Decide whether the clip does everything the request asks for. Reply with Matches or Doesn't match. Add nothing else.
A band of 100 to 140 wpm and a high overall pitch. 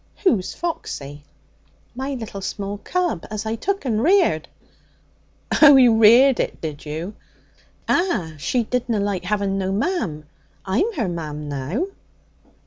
Matches